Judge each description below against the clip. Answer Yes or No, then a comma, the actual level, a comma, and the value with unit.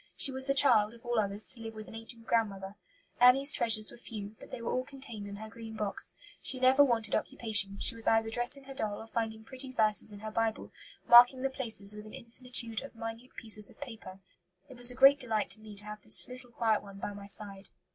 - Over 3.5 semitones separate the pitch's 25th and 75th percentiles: No, average, 2.9 semitones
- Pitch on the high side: Yes, high, 225 Hz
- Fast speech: Yes, fast, 235 wpm